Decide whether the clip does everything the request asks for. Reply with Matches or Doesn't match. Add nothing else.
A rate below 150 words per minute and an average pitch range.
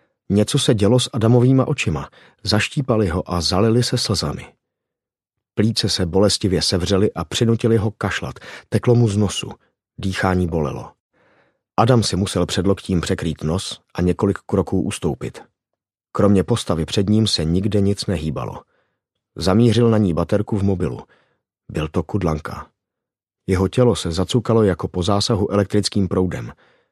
Matches